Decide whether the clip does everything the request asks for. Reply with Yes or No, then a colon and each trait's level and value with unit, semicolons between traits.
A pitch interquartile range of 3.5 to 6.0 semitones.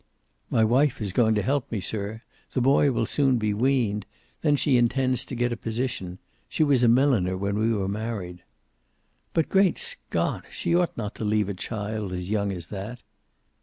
Yes: average, 4.3 semitones